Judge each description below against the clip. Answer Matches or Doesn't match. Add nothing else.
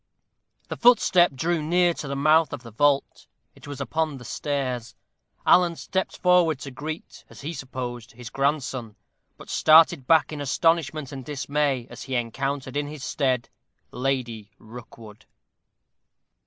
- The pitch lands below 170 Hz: Matches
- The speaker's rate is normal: Matches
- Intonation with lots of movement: Doesn't match